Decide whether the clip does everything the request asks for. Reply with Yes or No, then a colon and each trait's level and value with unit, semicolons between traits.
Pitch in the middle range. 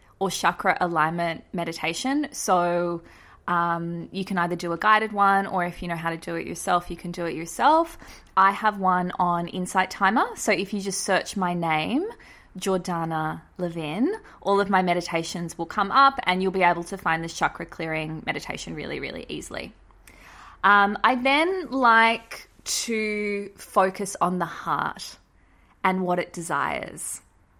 Yes: medium, 180 Hz